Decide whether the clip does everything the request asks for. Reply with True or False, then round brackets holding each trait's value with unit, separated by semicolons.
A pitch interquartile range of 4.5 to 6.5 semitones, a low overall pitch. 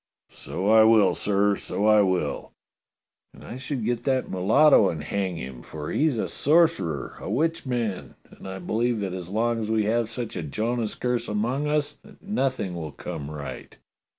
True (4.8 semitones; 110 Hz)